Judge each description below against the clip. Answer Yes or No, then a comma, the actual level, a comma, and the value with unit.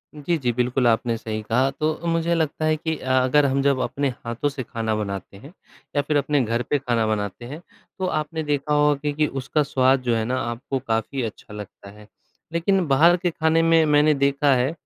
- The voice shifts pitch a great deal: No, average, 4.3 semitones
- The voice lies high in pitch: No, medium, 140 Hz